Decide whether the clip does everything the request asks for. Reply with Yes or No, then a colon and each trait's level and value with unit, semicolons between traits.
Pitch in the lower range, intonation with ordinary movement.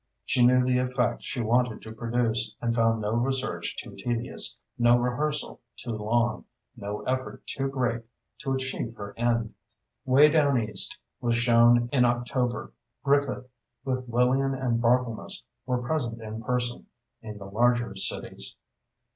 No: low, 120 Hz; narrow, 1.8 semitones